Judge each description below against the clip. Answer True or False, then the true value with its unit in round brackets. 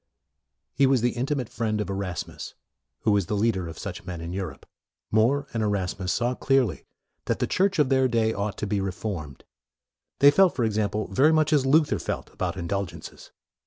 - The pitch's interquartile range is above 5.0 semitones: True (5.5 semitones)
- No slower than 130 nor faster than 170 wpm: False (185 wpm)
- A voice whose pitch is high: False (110 Hz)